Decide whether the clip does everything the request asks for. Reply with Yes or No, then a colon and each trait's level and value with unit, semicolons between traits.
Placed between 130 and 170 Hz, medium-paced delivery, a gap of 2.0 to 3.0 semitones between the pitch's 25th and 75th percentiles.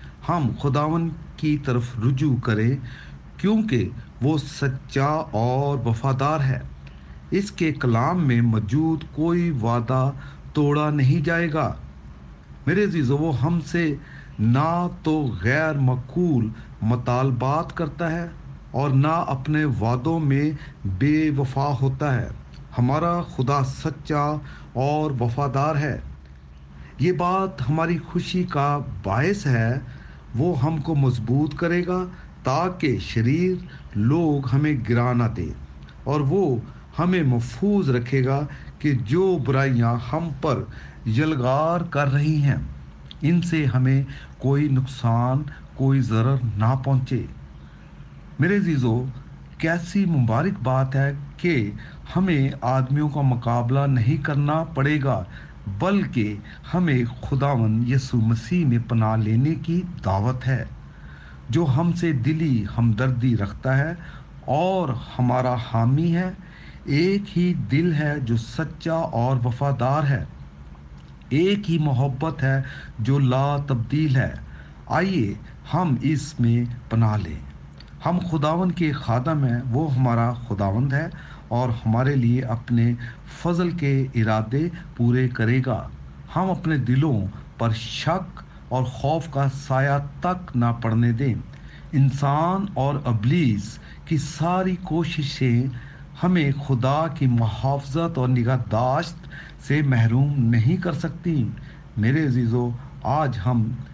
No: low, 135 Hz; average, 120 wpm; average, 4.5 semitones